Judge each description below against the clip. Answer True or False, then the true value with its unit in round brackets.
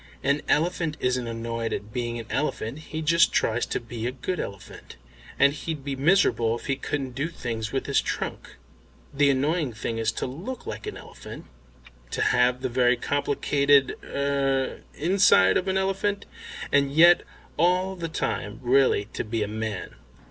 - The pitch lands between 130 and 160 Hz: True (135 Hz)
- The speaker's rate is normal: True (170 wpm)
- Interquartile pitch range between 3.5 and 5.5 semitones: True (5.0 semitones)